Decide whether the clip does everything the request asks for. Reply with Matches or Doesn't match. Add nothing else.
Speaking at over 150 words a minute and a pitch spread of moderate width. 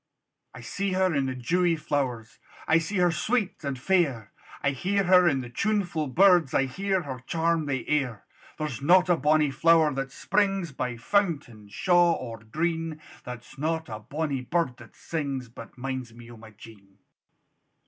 Doesn't match